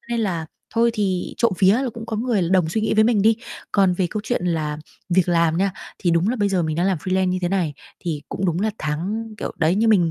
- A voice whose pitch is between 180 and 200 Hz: Yes, high, 190 Hz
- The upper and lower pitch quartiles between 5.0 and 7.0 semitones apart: No, average, 4.2 semitones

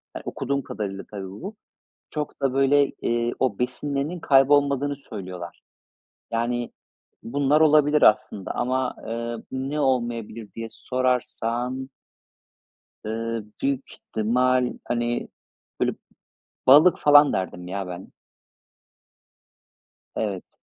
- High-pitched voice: No, low, 125 Hz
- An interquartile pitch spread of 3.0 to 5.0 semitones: Yes, average, 3.6 semitones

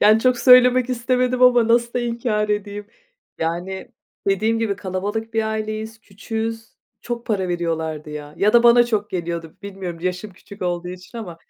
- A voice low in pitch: No, high, 215 Hz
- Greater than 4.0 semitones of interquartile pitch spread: Yes, average, 4.4 semitones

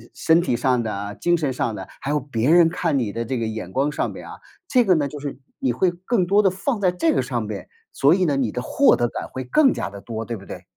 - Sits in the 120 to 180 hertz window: Yes, medium, 140 Hz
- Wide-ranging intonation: Yes, wide, 7.1 semitones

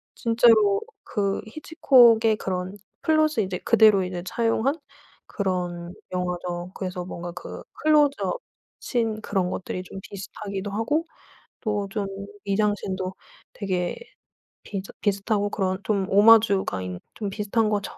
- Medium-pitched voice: No, high, 200 Hz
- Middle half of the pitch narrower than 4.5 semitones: Yes, average, 3.2 semitones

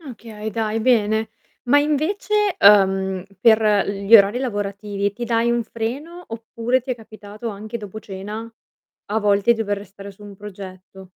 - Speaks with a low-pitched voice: No, high, 215 Hz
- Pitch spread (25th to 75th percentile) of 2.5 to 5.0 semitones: Yes, average, 2.8 semitones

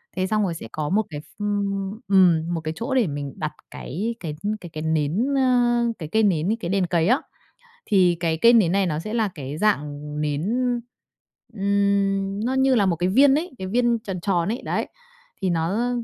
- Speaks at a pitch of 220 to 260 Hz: No, high, 195 Hz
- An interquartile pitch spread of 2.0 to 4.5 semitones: No, average, 5.3 semitones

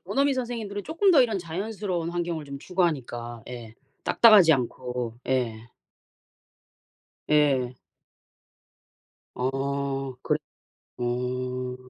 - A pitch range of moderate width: No, wide, 7.3 semitones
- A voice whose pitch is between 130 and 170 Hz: Yes, medium, 140 Hz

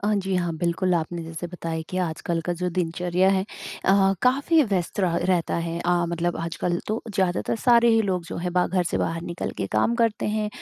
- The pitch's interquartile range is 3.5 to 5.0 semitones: No, narrow, 2.4 semitones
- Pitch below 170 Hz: No, medium, 180 Hz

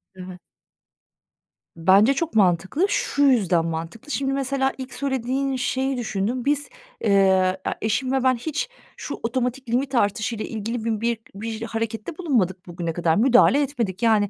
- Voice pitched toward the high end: Yes, high, 230 Hz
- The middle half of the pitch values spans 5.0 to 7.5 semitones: Yes, average, 5.3 semitones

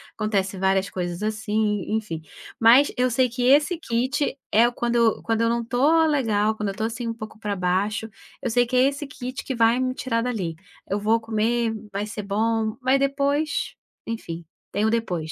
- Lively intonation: No, average, 3.2 semitones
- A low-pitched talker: No, high, 225 Hz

